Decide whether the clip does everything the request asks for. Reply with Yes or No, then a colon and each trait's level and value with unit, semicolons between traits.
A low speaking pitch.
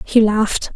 No: high, 215 Hz